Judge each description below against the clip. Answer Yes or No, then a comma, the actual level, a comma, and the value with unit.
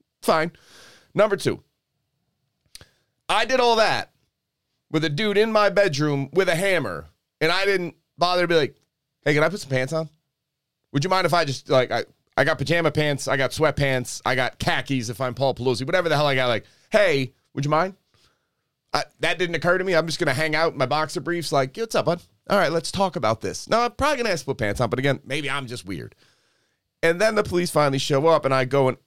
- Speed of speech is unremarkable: No, fast, 240 wpm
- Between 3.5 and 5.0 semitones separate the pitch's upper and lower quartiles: Yes, average, 4.6 semitones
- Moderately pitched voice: Yes, medium, 155 Hz